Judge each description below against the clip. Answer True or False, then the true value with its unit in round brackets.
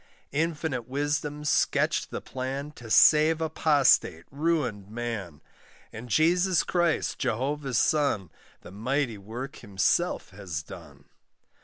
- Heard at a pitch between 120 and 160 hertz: True (135 Hz)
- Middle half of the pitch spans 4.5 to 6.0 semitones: True (5.5 semitones)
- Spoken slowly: True (110 wpm)